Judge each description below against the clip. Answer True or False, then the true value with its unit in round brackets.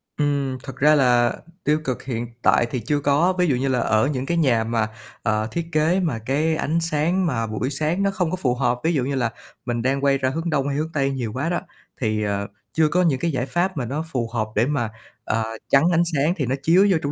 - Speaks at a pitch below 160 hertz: True (140 Hz)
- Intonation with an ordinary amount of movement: True (4.6 semitones)